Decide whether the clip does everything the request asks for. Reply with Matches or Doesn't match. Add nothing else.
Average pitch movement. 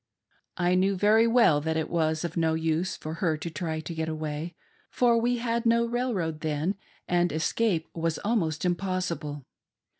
Matches